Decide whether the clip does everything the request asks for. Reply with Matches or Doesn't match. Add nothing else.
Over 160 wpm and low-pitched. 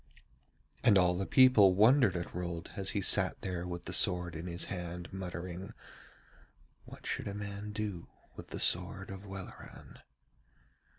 Doesn't match